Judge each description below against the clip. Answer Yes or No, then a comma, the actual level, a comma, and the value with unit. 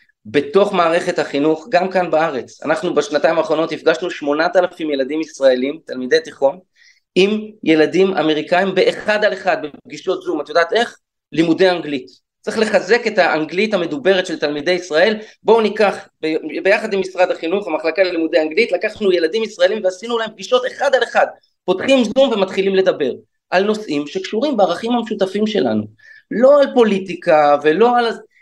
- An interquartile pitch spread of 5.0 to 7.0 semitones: Yes, average, 5.3 semitones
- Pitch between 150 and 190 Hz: Yes, medium, 185 Hz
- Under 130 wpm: No, fast, 150 wpm